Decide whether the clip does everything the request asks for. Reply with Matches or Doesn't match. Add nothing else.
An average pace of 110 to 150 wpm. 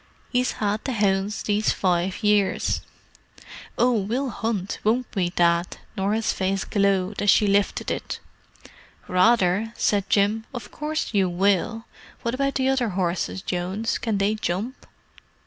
Matches